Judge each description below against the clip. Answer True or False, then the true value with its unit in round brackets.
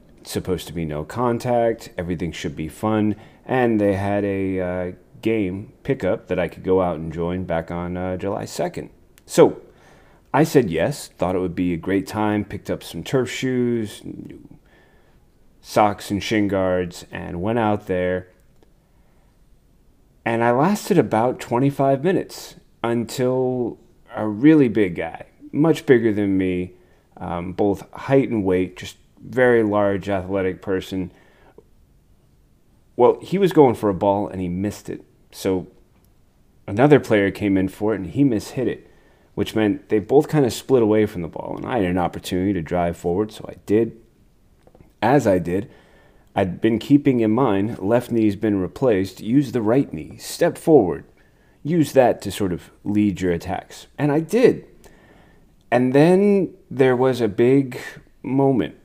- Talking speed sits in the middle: True (160 wpm)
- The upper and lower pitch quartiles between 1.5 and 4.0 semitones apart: False (4.9 semitones)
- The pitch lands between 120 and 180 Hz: False (105 Hz)